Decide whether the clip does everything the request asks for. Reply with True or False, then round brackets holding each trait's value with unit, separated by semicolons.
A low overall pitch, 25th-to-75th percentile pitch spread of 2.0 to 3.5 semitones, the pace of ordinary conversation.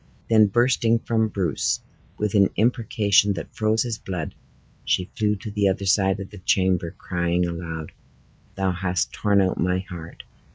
True (95 Hz; 3.1 semitones; 160 wpm)